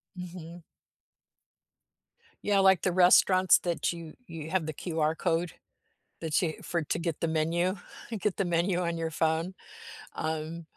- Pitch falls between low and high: Yes, medium, 170 Hz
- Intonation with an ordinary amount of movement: No, narrow, 2.0 semitones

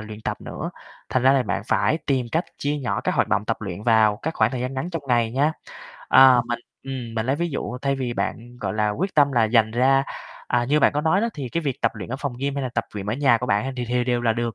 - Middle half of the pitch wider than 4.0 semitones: No, average, 3.1 semitones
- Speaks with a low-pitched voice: Yes, low, 125 Hz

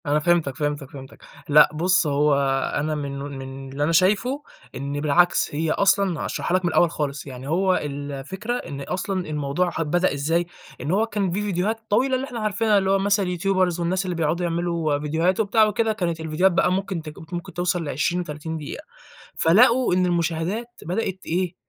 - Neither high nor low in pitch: Yes, medium, 175 Hz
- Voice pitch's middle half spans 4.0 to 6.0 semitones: Yes, average, 4.3 semitones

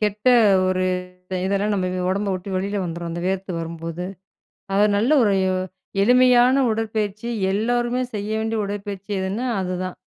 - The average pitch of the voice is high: Yes, high, 200 Hz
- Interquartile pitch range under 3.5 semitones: Yes, average, 3.0 semitones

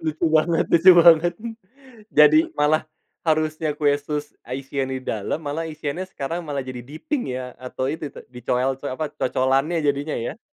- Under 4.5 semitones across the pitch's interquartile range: Yes, average, 3.1 semitones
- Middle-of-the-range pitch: Yes, medium, 150 Hz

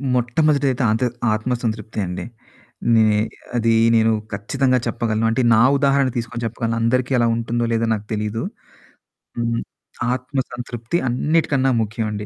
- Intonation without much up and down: Yes, narrow, 2.3 semitones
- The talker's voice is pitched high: No, low, 115 Hz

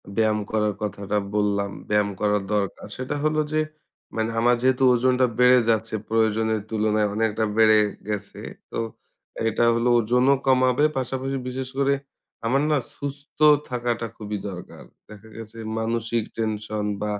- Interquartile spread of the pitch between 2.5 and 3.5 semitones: Yes, average, 3.1 semitones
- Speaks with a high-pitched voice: No, low, 110 Hz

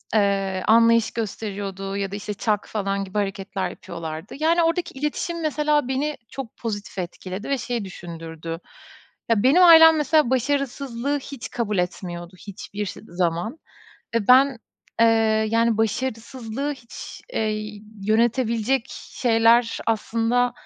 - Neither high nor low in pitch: No, high, 225 Hz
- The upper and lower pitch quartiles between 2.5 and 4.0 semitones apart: No, average, 4.8 semitones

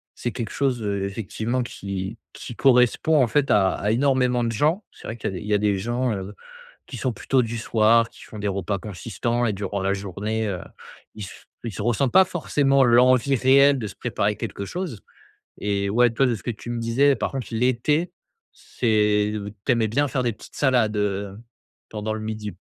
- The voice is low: Yes, low, 115 Hz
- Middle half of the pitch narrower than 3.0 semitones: No, average, 3.7 semitones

